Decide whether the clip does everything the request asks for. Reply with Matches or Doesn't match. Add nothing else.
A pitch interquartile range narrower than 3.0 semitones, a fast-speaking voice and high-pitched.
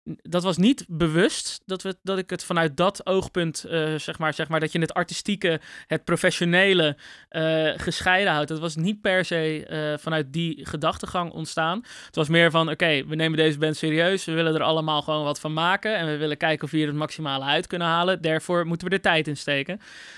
Doesn't match